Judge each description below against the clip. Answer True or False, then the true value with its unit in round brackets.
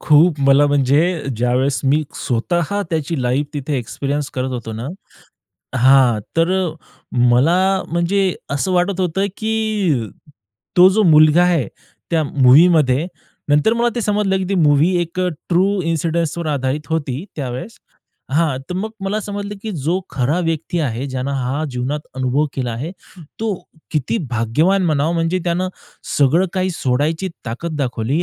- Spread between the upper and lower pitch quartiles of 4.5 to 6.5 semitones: True (5.2 semitones)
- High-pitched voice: False (155 Hz)